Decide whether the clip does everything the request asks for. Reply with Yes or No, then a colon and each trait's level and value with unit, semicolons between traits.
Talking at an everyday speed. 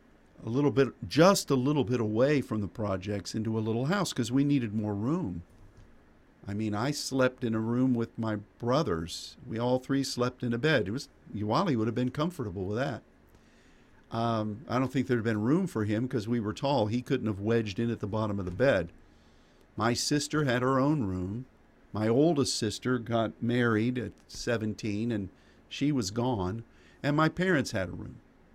Yes: average, 195 wpm